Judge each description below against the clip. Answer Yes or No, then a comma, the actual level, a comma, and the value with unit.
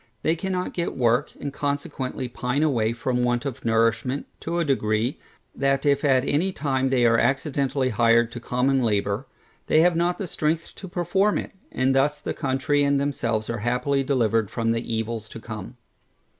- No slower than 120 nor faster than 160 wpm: No, average, 175 wpm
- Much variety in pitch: No, average, 3.7 semitones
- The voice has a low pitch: Yes, low, 130 Hz